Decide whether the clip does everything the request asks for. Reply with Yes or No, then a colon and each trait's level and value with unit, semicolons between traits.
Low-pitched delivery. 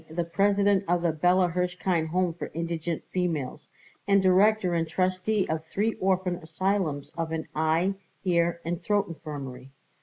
No: medium, 175 Hz